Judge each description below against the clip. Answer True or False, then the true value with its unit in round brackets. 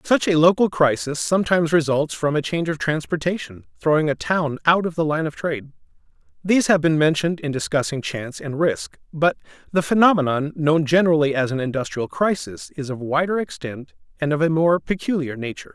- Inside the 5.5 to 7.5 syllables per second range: True (5.8 syllables/s)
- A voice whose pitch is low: False (150 Hz)